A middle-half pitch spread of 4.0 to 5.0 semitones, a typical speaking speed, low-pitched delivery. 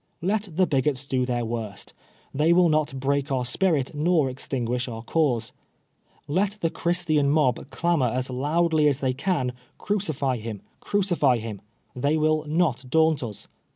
No: average, 4.4 semitones; average, 165 wpm; medium, 145 Hz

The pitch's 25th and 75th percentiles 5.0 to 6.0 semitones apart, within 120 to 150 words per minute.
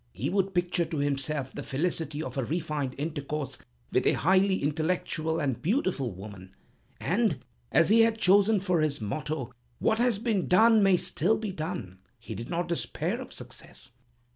No: average, 5.3 semitones; average, 165 wpm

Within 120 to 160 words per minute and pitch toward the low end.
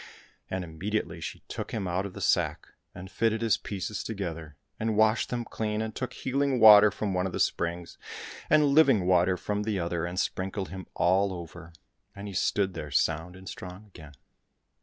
No: average, 185 wpm; very low, 95 Hz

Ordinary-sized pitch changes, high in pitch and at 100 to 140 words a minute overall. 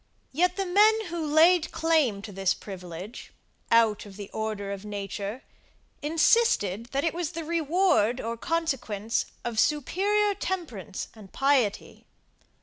No: wide, 8.5 semitones; very high, 265 Hz; slow, 135 wpm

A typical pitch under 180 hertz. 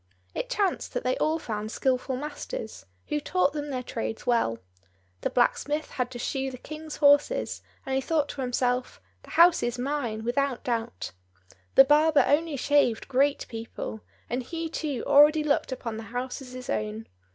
No: very high, 265 Hz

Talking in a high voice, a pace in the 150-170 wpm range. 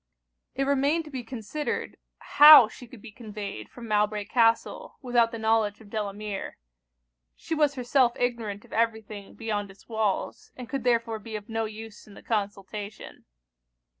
Yes: high, 225 Hz; average, 165 wpm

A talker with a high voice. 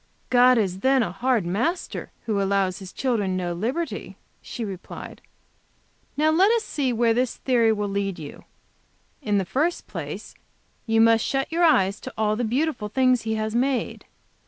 Yes: high, 225 Hz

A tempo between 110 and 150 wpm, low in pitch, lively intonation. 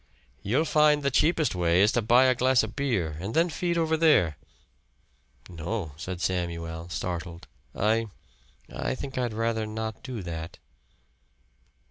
Yes: average, 145 wpm; low, 110 Hz; wide, 7.1 semitones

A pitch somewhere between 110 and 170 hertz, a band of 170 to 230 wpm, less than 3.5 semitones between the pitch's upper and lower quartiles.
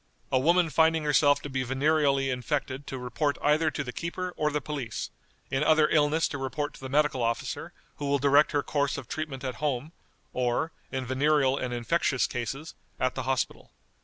Yes: medium, 140 Hz; average, 190 wpm; narrow, 2.5 semitones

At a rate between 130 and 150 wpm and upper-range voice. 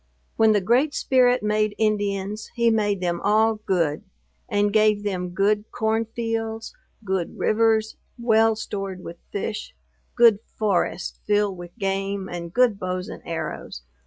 Yes: average, 140 wpm; high, 210 Hz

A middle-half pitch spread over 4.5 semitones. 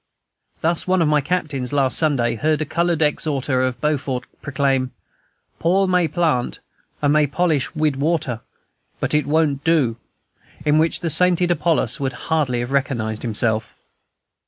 No: average, 3.8 semitones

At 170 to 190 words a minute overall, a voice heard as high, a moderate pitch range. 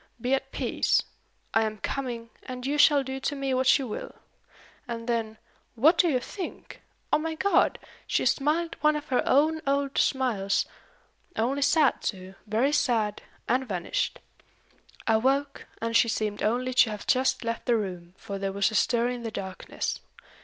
Yes: average, 175 wpm; very high, 250 Hz; average, 4.1 semitones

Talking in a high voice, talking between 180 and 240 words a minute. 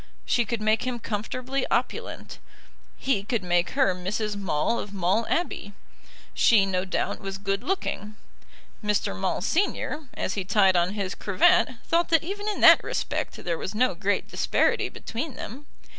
No: high, 210 Hz; average, 160 wpm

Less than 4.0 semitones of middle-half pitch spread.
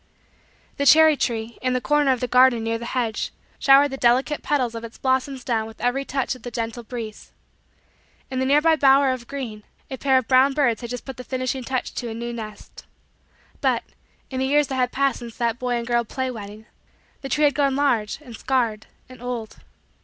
Yes: narrow, 2.5 semitones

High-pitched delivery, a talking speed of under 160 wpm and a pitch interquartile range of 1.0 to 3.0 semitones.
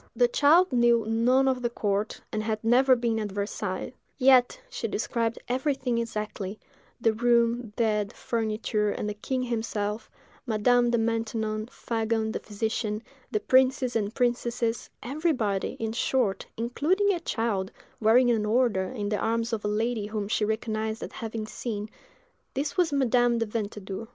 Yes: high, 230 Hz; average, 150 wpm; narrow, 2.4 semitones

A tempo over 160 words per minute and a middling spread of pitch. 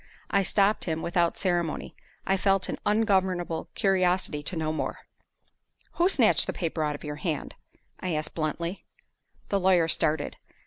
No: average, 150 wpm; average, 3.4 semitones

